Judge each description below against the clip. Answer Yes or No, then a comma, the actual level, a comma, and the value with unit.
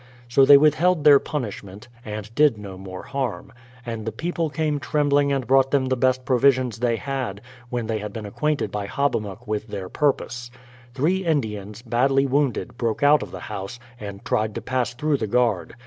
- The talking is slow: No, average, 185 wpm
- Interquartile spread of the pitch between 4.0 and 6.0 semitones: Yes, average, 4.8 semitones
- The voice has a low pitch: Yes, low, 125 Hz